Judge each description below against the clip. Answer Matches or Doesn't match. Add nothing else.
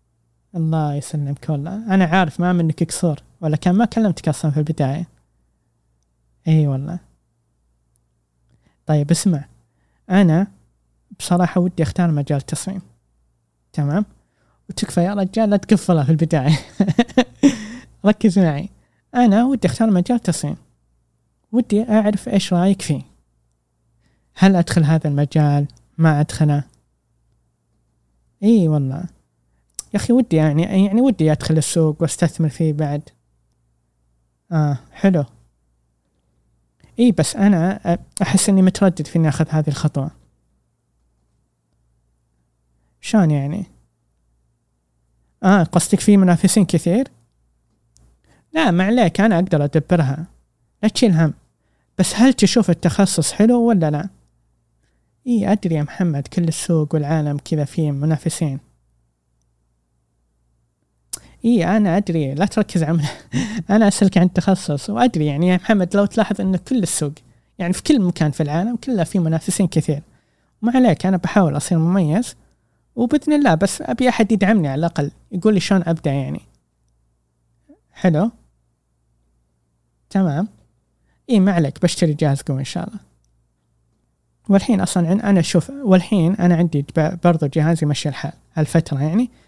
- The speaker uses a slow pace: Doesn't match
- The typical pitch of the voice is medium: Matches